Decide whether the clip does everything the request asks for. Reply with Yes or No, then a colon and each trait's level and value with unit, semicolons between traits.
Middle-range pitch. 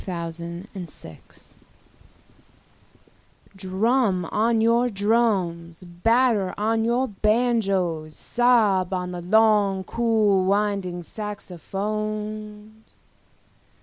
No: high, 205 Hz